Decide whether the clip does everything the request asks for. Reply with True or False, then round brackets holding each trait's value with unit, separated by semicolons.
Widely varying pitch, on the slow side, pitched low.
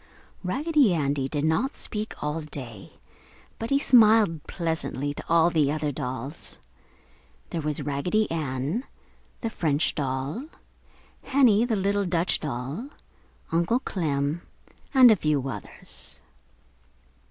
False (7.1 semitones; 120 wpm; 160 Hz)